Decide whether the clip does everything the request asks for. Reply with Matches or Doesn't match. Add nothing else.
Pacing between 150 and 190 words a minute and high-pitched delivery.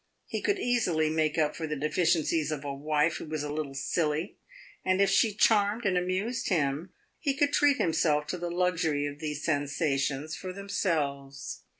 Doesn't match